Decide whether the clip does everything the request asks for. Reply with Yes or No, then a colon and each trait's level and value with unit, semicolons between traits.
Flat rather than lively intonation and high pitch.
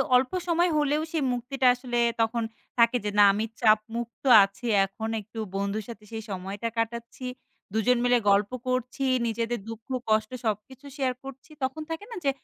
No: average, 3.1 semitones; high, 235 Hz